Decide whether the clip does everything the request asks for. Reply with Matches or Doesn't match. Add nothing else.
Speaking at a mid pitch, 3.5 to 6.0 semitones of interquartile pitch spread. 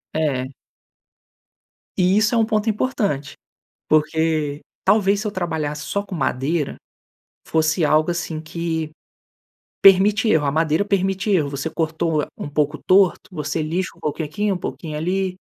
Matches